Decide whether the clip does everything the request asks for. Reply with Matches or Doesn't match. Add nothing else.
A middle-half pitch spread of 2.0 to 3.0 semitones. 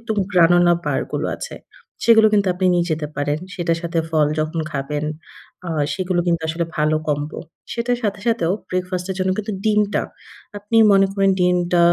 Doesn't match